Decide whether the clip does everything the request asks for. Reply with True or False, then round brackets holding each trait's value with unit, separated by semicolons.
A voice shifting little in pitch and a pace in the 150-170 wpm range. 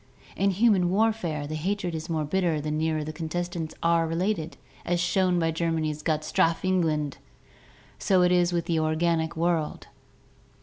True (2.2 semitones; 160 wpm)